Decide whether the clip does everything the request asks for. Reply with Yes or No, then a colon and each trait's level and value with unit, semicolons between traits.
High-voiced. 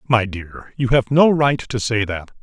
No: low, 120 Hz